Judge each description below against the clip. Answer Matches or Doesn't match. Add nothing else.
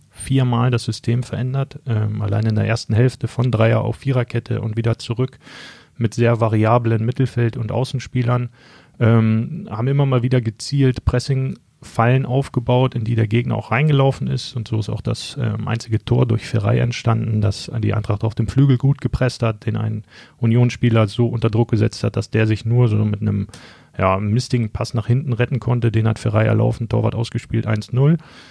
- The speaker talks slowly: Doesn't match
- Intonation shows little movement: Matches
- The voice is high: Doesn't match